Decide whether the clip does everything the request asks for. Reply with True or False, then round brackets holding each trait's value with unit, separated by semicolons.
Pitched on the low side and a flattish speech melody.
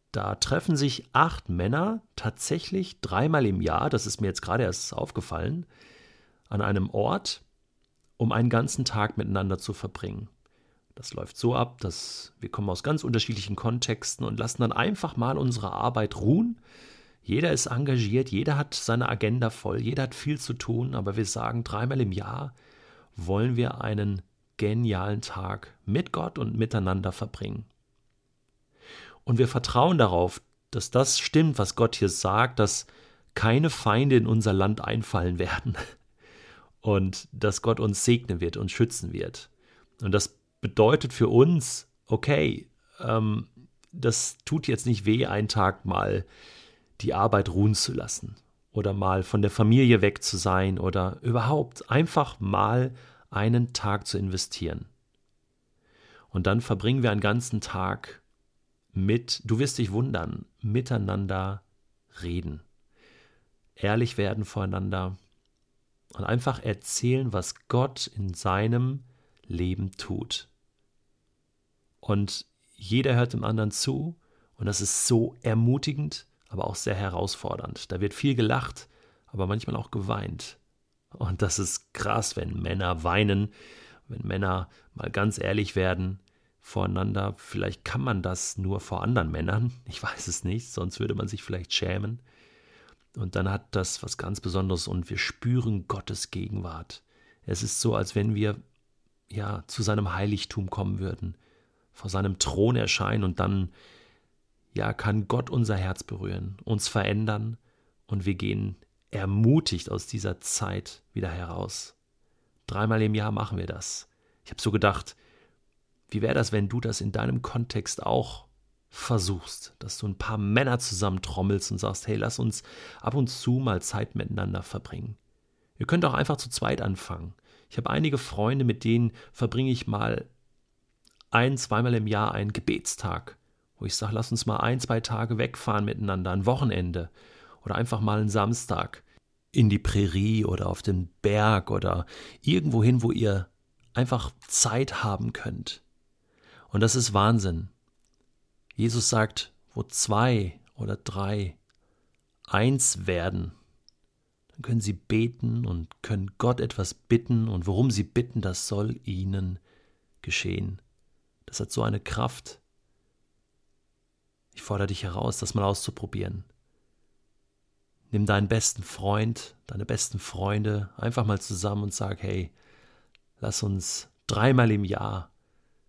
False (110 Hz; 3.3 semitones)